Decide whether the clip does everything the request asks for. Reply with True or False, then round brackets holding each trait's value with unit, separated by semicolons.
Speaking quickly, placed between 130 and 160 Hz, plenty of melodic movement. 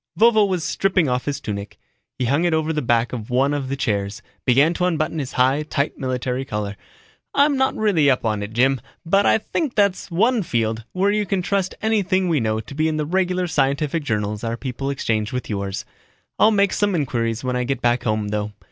True (215 wpm; 140 Hz; 7.7 semitones)